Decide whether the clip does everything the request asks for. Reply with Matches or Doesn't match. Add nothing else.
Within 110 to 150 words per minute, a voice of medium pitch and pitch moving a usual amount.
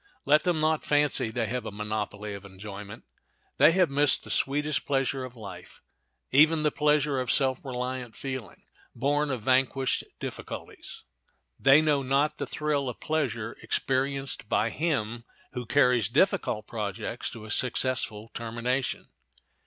Doesn't match